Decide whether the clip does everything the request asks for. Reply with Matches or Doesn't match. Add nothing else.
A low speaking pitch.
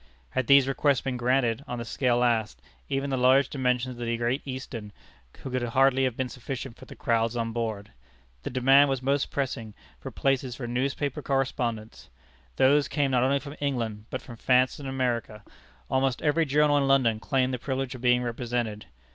Matches